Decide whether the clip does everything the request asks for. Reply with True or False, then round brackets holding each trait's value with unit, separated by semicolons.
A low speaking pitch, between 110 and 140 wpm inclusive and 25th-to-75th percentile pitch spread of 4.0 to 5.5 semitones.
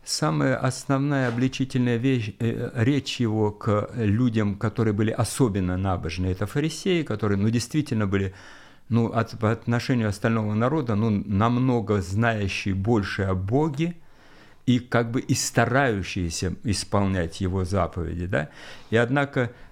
True (115 Hz; 130 wpm; 4.3 semitones)